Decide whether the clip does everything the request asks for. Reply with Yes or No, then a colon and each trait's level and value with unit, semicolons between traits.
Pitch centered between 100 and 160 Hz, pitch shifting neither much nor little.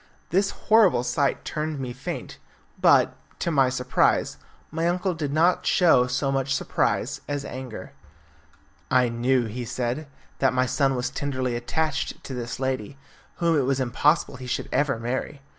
Yes: low, 135 Hz; average, 3.1 semitones